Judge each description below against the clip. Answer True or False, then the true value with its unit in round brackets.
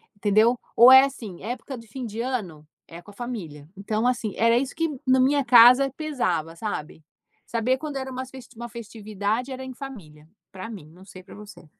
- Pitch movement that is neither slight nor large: True (4.4 semitones)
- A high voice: True (230 Hz)